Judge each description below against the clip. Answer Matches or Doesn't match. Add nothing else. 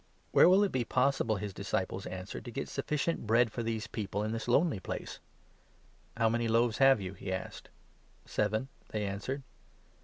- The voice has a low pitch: Matches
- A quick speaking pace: Matches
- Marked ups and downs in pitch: Doesn't match